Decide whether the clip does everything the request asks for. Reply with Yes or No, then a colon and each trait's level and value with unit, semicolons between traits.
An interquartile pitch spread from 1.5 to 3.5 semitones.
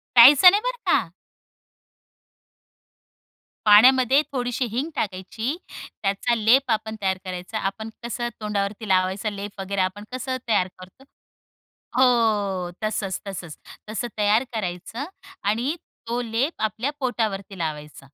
No: average, 4.1 semitones